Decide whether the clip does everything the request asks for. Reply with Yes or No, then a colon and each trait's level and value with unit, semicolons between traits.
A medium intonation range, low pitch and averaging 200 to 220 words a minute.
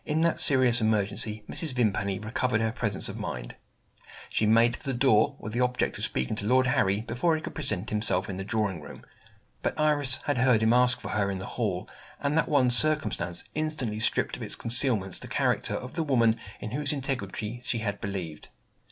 Yes: average, 3.9 semitones; low, 115 Hz; fast, 205 wpm